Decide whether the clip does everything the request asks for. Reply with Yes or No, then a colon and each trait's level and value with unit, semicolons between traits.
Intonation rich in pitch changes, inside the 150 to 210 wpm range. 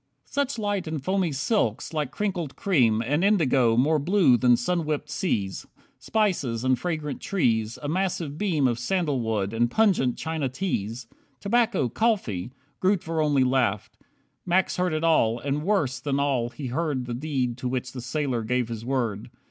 Yes: wide, 6.5 semitones; average, 165 wpm